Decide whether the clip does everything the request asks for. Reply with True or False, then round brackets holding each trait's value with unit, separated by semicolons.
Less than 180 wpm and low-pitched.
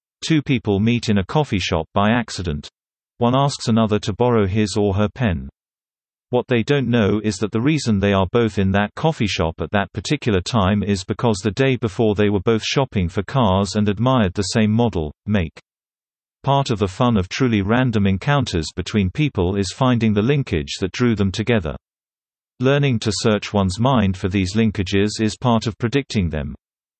False (190 wpm; 105 Hz)